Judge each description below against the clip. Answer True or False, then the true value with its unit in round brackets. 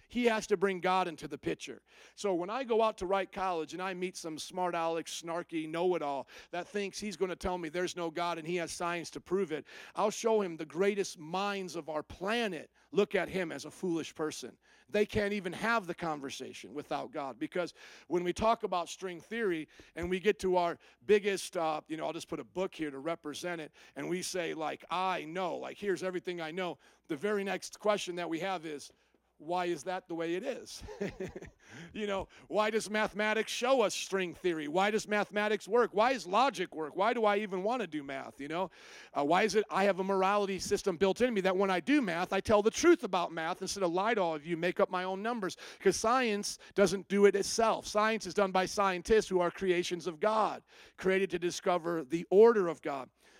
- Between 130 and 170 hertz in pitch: False (185 Hz)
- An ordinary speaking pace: False (230 wpm)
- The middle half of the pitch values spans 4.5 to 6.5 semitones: False (3.2 semitones)